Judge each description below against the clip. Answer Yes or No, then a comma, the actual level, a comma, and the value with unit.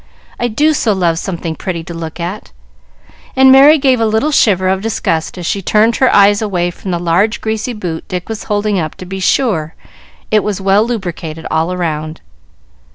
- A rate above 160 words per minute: Yes, average, 190 wpm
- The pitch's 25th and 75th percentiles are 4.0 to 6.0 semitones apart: Yes, average, 4.3 semitones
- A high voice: Yes, high, 195 Hz